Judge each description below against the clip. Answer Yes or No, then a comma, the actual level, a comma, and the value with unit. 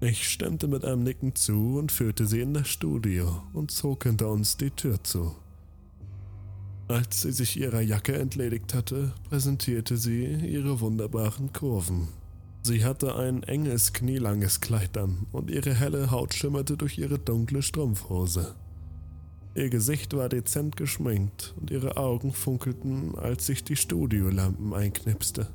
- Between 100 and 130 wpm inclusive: No, average, 145 wpm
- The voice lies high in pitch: No, low, 120 Hz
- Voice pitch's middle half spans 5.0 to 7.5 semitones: Yes, wide, 5.5 semitones